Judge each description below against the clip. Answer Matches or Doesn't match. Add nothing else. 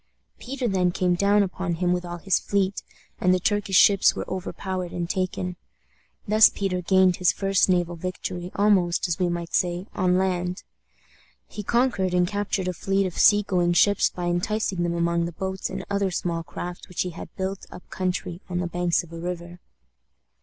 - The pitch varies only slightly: Matches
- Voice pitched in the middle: Matches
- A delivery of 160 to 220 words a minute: Matches